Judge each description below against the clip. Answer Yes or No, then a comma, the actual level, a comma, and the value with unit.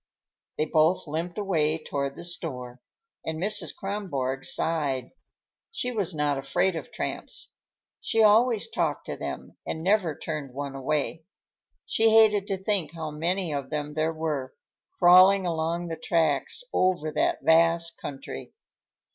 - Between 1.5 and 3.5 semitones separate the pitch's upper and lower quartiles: No, average, 4.0 semitones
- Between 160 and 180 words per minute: No, average, 140 wpm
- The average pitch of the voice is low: No, medium, 165 Hz